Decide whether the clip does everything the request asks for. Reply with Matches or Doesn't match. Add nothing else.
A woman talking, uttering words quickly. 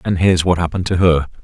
Doesn't match